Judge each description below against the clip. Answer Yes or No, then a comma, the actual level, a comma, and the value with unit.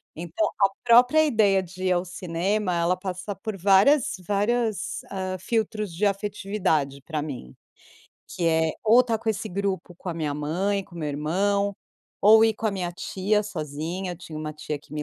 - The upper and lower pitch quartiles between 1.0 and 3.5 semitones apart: No, average, 3.9 semitones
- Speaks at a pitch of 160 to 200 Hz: Yes, high, 190 Hz